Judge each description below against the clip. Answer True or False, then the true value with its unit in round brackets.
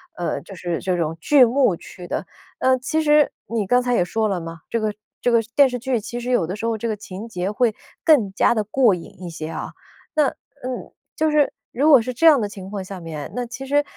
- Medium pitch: False (225 Hz)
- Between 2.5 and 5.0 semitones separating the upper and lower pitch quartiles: False (5.5 semitones)